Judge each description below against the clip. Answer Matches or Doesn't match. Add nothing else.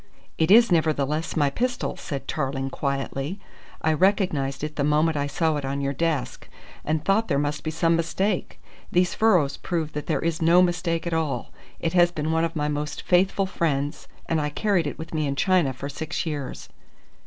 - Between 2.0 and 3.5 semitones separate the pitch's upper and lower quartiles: Matches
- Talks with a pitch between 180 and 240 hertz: Doesn't match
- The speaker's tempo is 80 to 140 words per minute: Doesn't match